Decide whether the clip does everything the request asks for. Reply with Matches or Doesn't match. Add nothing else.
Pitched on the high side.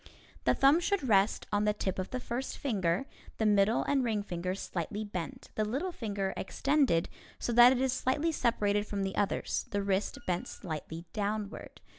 Matches